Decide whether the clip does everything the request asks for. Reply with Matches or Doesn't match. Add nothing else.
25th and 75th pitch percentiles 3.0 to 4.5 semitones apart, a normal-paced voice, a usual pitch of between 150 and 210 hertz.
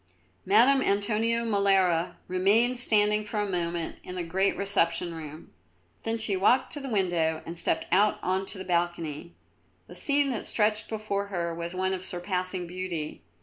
Matches